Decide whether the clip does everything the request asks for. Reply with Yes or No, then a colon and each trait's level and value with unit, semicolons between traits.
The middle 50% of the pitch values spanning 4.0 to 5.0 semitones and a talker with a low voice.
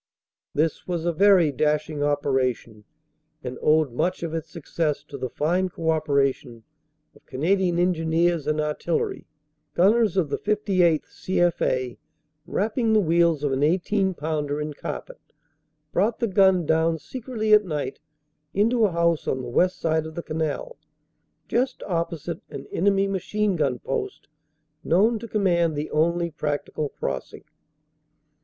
No: average, 4.3 semitones; medium, 165 Hz